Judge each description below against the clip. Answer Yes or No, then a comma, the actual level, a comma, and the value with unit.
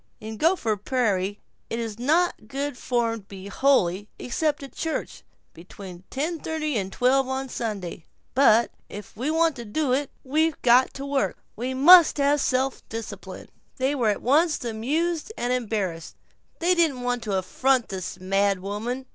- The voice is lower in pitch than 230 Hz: No, very high, 250 Hz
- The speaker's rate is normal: Yes, average, 170 wpm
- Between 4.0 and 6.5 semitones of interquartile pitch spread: Yes, wide, 5.4 semitones